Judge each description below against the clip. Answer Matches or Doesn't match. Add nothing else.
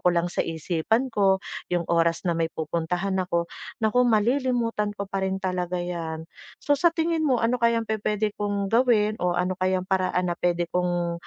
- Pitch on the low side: Doesn't match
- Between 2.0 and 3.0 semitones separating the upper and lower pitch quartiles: Doesn't match